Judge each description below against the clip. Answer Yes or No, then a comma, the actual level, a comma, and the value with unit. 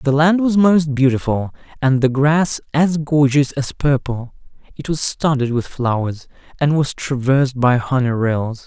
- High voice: No, low, 135 Hz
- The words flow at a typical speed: Yes, average, 160 wpm